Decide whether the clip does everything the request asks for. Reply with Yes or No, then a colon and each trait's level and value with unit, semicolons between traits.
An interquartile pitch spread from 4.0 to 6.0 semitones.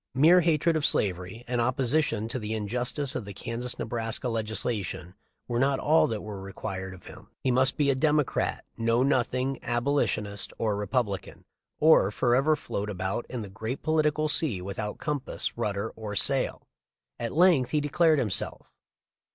Yes: average, 5.1 semitones